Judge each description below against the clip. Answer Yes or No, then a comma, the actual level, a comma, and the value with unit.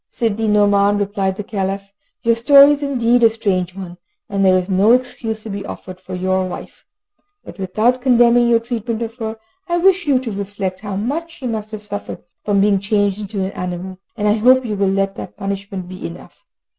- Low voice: No, high, 205 Hz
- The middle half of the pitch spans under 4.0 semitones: Yes, average, 3.2 semitones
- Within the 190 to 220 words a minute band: Yes, average, 200 wpm